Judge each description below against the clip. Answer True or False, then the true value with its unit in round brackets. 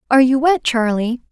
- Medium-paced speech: True (185 wpm)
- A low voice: False (255 Hz)